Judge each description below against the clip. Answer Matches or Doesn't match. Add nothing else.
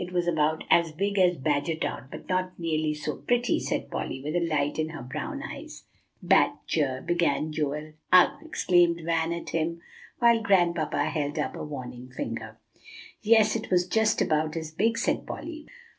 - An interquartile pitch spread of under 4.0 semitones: Matches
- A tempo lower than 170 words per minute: Doesn't match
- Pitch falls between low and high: Matches